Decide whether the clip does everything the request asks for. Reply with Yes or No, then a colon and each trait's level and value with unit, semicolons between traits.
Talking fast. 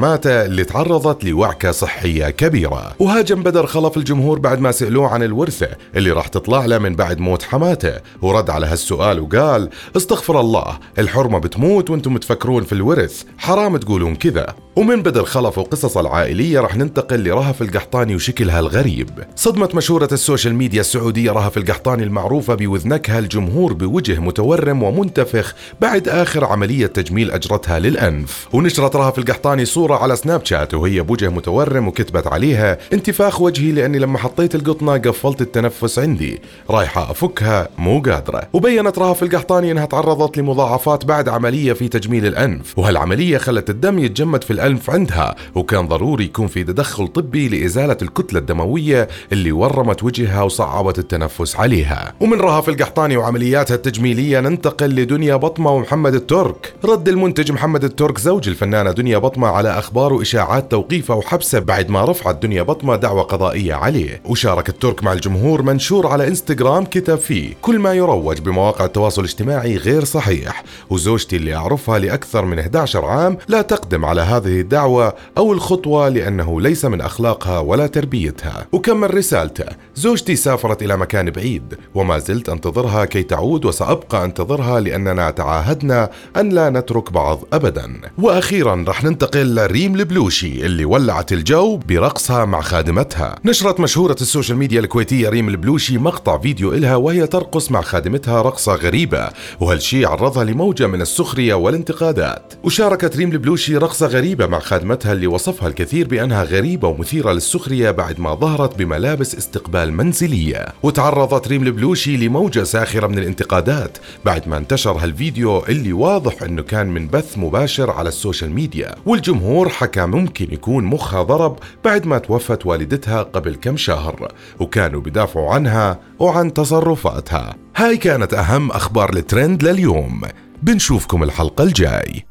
Yes: fast, 145 wpm